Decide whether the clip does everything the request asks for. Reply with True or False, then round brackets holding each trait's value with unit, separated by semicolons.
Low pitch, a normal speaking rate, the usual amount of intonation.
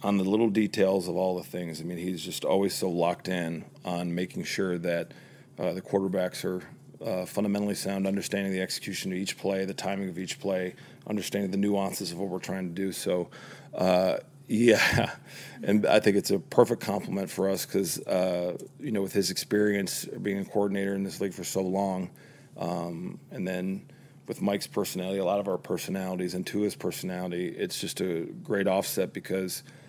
False (95 Hz; 195 wpm; 1.5 semitones)